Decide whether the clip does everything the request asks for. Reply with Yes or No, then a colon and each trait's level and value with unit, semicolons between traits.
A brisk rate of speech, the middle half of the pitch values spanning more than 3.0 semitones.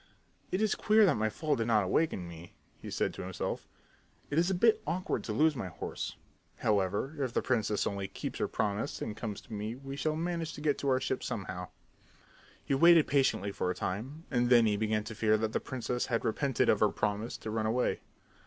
Yes: fast, 220 wpm; wide, 5.6 semitones